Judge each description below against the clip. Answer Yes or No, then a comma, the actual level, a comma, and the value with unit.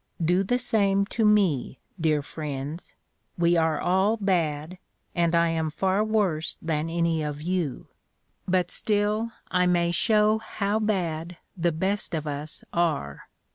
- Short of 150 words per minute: Yes, average, 140 wpm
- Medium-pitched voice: Yes, medium, 175 Hz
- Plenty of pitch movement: No, average, 4.0 semitones